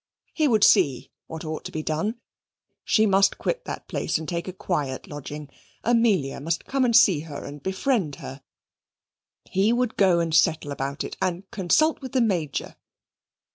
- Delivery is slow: No, average, 175 wpm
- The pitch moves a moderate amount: No, wide, 6.6 semitones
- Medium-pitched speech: Yes, medium, 175 Hz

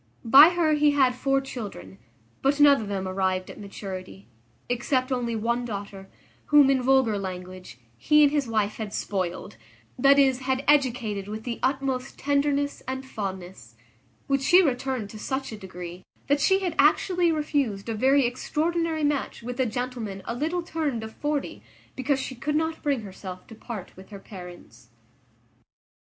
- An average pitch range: No, wide, 6.0 semitones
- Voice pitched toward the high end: Yes, very high, 250 Hz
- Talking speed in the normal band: Yes, average, 165 wpm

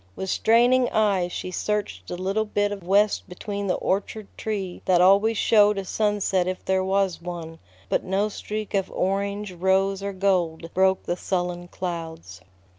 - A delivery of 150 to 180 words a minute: Yes, average, 165 wpm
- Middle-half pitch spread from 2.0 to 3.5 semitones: Yes, narrow, 2.4 semitones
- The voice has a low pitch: No, high, 190 Hz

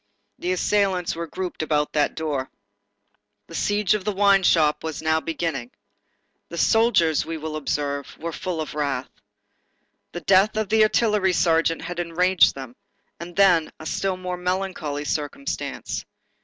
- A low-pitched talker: No, medium, 170 Hz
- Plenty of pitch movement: No, average, 3.4 semitones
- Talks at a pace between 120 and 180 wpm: Yes, average, 150 wpm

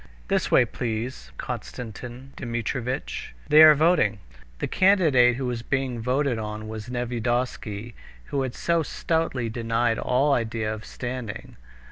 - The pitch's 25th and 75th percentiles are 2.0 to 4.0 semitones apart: Yes, average, 2.9 semitones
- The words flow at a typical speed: No, slow, 130 wpm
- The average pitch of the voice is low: Yes, low, 125 Hz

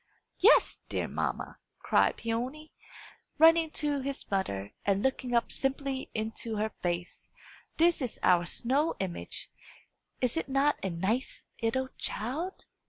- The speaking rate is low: Yes, slow, 130 wpm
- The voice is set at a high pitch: Yes, very high, 255 Hz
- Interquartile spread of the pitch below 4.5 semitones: No, wide, 5.6 semitones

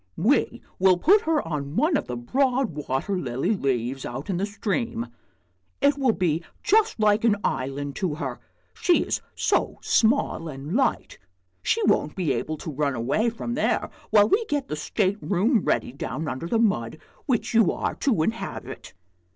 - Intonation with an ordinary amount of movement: No, wide, 8.6 semitones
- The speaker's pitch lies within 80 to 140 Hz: No, high, 190 Hz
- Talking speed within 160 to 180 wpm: Yes, average, 175 wpm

